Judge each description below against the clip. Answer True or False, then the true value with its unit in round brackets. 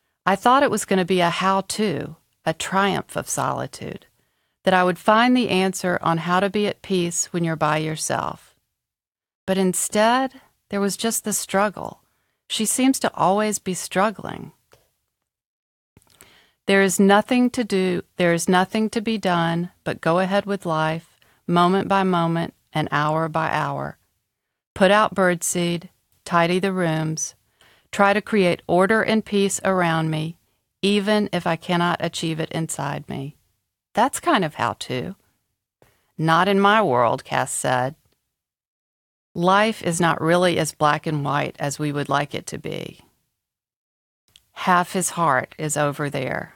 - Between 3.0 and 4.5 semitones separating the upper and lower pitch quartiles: True (3.6 semitones)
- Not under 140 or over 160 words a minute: True (155 wpm)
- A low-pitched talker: False (180 Hz)